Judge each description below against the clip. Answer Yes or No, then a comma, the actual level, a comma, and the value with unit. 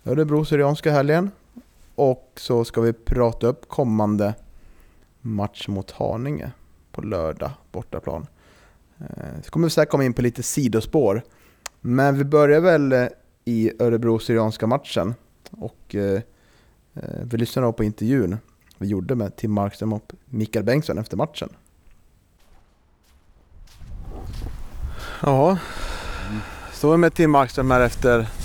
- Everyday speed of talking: No, slow, 120 wpm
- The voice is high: No, low, 115 Hz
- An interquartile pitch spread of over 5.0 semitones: Yes, wide, 5.4 semitones